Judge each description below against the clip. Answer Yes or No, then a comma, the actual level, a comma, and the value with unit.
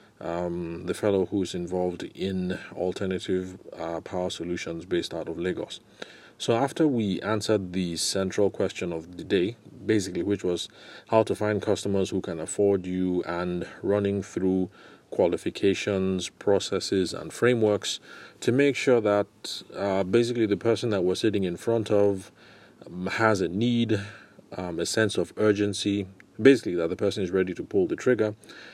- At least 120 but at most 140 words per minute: No, average, 155 wpm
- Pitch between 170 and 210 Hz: No, low, 100 Hz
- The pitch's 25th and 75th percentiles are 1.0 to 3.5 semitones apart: Yes, average, 2.8 semitones